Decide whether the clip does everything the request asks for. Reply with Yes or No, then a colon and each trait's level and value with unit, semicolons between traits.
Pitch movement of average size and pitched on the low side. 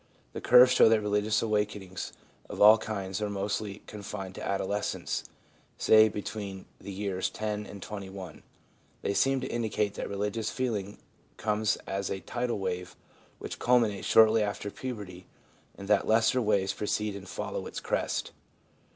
No: narrow, 1.9 semitones; low, 105 Hz